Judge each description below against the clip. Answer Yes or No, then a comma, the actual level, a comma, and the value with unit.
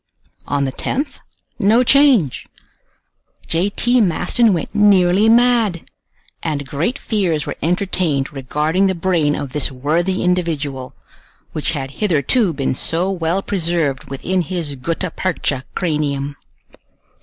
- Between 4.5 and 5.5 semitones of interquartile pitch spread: Yes, average, 5.2 semitones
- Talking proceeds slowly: Yes, slow, 120 wpm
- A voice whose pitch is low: No, medium, 170 Hz